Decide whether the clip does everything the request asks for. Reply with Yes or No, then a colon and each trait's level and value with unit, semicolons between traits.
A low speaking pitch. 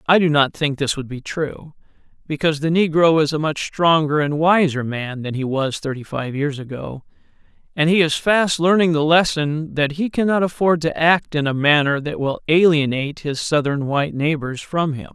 No: medium, 155 Hz